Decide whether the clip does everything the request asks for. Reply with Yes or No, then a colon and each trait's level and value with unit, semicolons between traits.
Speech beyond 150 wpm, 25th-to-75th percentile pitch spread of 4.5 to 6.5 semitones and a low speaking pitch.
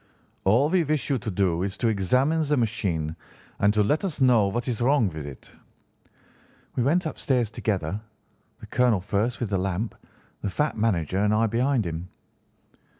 Yes: average, 175 wpm; average, 4.9 semitones; low, 110 Hz